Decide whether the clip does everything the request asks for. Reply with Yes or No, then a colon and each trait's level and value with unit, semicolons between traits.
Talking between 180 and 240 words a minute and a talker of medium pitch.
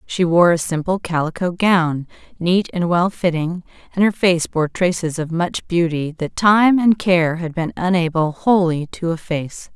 No: average, 170 wpm; medium, 175 Hz